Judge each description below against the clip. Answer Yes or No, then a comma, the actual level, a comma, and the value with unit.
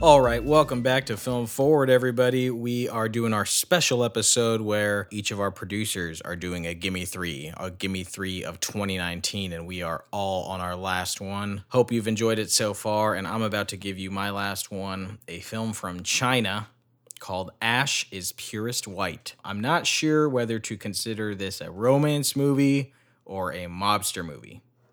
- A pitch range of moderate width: Yes, average, 4.2 semitones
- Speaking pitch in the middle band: No, low, 105 Hz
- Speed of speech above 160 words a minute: Yes, average, 180 wpm